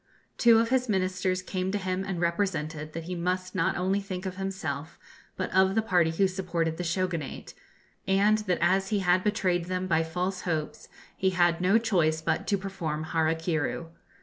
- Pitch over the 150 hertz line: Yes, medium, 185 Hz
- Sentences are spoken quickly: No, average, 185 wpm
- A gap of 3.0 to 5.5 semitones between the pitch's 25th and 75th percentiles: No, narrow, 2.5 semitones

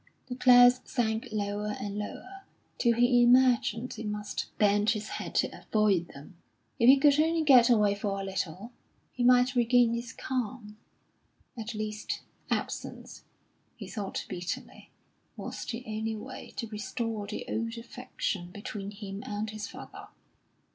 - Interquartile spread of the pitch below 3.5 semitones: Yes, average, 3.0 semitones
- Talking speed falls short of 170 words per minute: Yes, average, 145 wpm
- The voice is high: Yes, high, 220 Hz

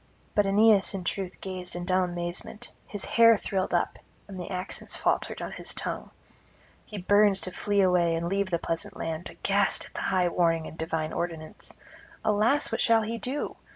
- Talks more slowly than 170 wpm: No, average, 185 wpm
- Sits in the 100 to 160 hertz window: No, medium, 185 Hz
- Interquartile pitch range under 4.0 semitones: Yes, average, 2.9 semitones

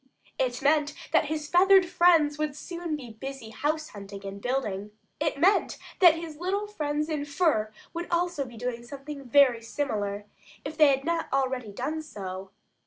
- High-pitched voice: Yes, very high, 290 Hz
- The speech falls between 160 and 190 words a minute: Yes, average, 170 wpm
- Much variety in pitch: No, average, 4.9 semitones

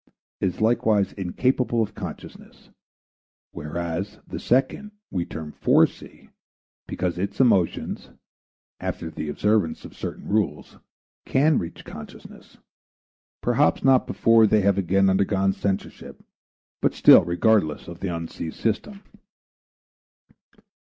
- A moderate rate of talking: No, slow, 110 wpm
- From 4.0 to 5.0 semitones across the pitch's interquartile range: Yes, average, 4.4 semitones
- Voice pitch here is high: No, low, 100 Hz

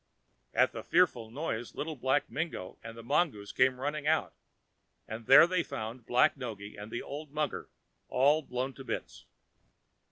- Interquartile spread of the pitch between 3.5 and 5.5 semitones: Yes, average, 4.9 semitones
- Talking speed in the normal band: Yes, average, 160 wpm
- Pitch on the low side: Yes, low, 130 Hz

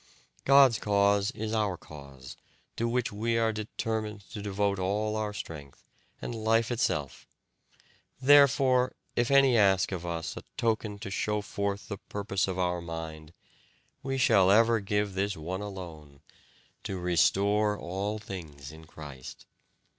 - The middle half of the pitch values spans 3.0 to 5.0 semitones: Yes, average, 3.9 semitones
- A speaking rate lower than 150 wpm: Yes, average, 140 wpm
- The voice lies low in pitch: Yes, low, 100 Hz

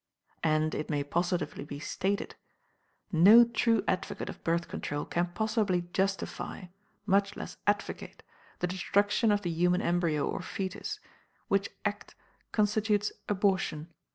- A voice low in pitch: No, medium, 185 Hz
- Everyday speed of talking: No, slow, 125 wpm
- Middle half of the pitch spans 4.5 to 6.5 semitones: No, average, 3.2 semitones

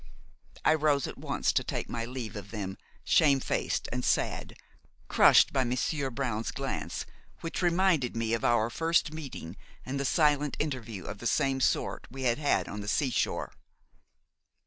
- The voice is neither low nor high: No, low, 130 Hz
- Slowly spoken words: No, average, 165 wpm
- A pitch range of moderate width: Yes, average, 4.2 semitones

